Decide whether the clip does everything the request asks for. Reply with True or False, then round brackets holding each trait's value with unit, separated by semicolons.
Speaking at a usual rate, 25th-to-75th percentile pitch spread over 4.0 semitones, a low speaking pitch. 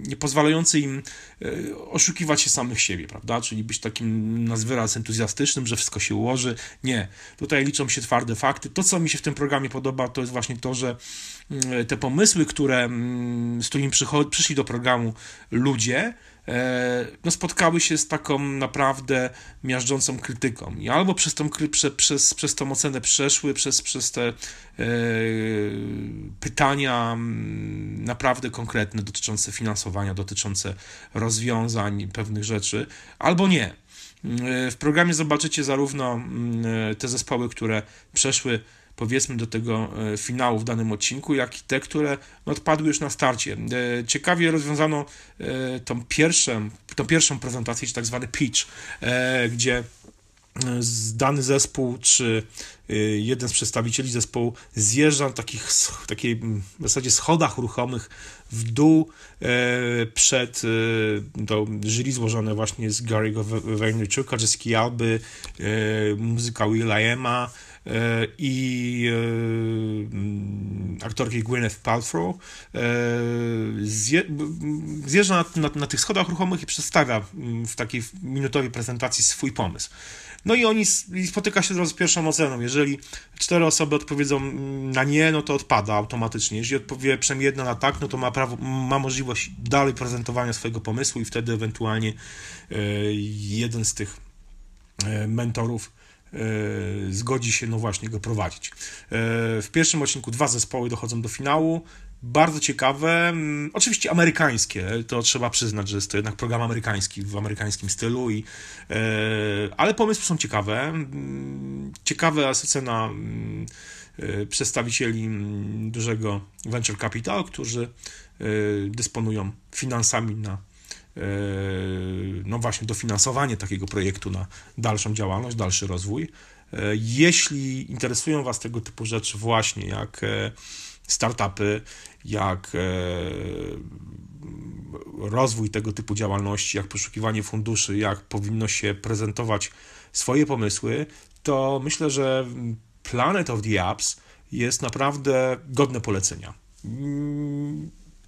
True (120 wpm; 4.4 semitones; 120 Hz)